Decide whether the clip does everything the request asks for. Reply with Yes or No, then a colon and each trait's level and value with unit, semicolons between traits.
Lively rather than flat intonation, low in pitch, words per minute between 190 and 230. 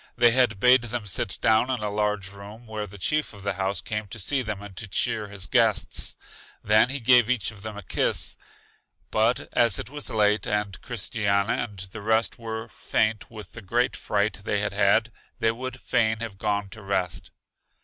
No: narrow, 2.5 semitones; low, 110 Hz; average, 200 wpm